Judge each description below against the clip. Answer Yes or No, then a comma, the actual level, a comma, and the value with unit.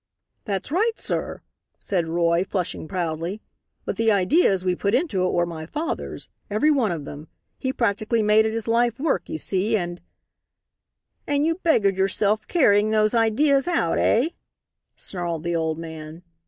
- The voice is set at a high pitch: Yes, high, 205 Hz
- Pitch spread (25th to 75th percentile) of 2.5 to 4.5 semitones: No, wide, 5.4 semitones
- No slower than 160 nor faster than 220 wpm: Yes, average, 165 wpm